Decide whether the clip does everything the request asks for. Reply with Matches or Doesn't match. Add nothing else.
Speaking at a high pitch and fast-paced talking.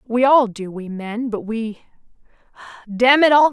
Doesn't match